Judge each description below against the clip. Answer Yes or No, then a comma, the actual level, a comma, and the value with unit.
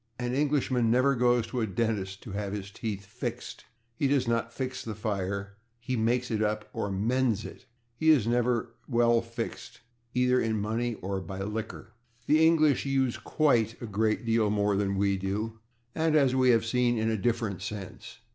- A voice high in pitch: No, low, 115 Hz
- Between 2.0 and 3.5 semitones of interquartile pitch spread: Yes, average, 3.1 semitones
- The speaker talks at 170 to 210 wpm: Yes, average, 185 wpm